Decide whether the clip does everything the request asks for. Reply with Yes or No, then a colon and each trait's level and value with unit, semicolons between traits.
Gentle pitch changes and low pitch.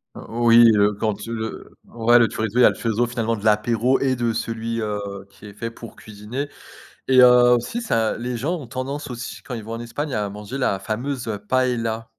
Yes: narrow, 2.1 semitones; low, 115 Hz